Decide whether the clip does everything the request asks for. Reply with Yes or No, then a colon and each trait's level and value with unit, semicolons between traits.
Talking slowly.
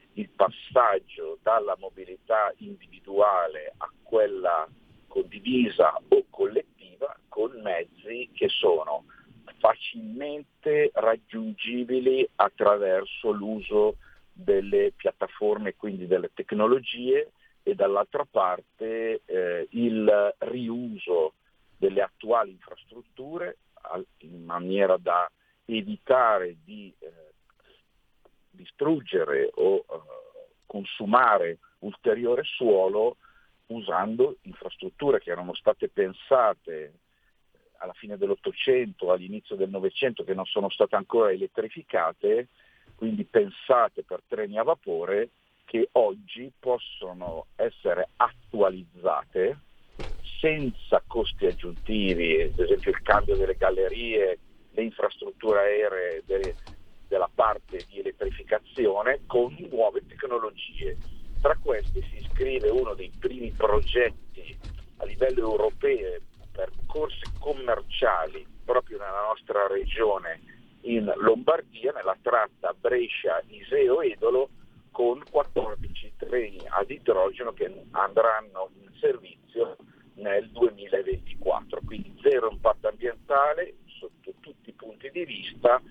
Yes: slow, 95 wpm